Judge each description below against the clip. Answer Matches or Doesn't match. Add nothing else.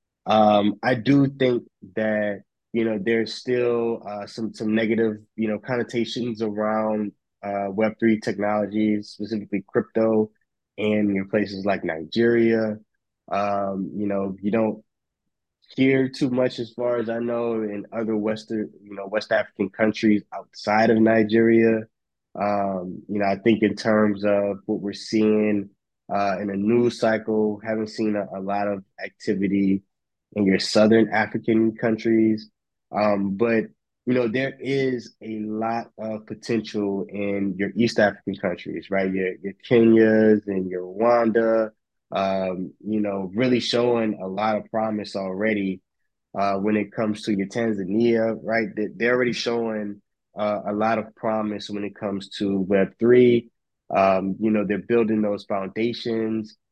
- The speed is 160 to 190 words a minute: Doesn't match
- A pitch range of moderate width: Doesn't match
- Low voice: Matches